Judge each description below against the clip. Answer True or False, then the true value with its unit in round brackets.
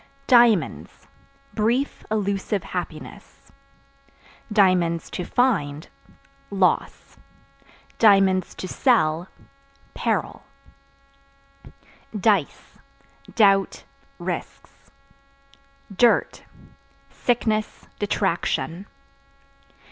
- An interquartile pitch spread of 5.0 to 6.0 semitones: False (3.6 semitones)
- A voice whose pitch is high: True (195 Hz)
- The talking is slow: True (50 wpm)